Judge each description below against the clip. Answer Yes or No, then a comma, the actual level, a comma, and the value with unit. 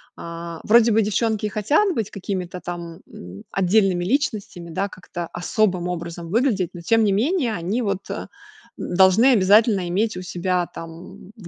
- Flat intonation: No, average, 3.8 semitones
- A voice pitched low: No, high, 190 Hz